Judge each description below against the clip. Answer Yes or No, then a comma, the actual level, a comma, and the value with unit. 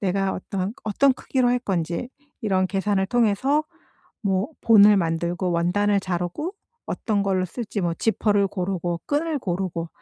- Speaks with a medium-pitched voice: No, high, 195 Hz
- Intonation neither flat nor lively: Yes, average, 3.6 semitones